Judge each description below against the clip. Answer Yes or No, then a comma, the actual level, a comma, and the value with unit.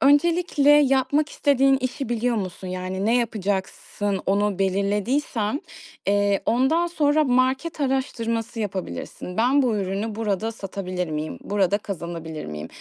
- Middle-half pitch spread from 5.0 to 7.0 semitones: Yes, wide, 5.6 semitones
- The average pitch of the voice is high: Yes, high, 220 Hz